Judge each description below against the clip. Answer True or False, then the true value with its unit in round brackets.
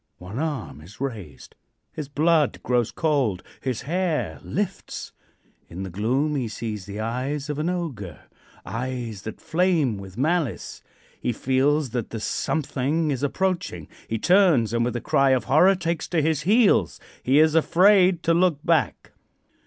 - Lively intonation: True (6.3 semitones)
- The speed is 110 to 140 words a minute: False (155 wpm)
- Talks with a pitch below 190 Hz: True (135 Hz)